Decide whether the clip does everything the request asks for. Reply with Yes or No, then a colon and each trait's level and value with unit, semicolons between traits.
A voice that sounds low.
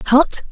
No: very high, 270 Hz